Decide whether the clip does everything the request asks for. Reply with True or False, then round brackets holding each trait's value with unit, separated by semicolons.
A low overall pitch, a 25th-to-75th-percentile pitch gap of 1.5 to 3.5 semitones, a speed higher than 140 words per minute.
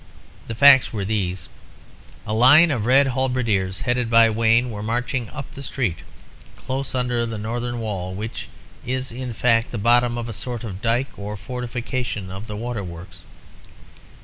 True (115 Hz; 3.0 semitones; 160 wpm)